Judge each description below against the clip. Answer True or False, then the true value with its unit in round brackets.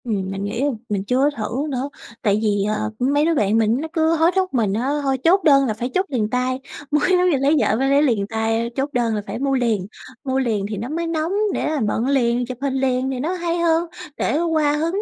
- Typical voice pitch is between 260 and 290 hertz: True (265 Hz)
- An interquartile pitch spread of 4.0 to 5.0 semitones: False (5.4 semitones)